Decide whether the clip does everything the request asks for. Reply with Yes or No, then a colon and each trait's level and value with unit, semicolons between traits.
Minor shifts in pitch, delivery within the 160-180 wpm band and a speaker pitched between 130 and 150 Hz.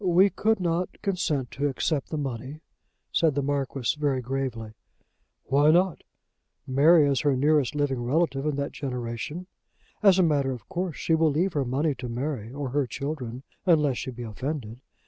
No: average, 3.5 semitones; average, 170 wpm; medium, 140 Hz